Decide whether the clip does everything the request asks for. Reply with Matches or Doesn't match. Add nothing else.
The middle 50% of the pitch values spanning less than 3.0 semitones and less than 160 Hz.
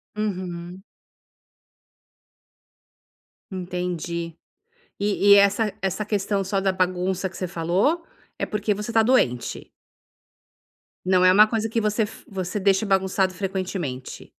Doesn't match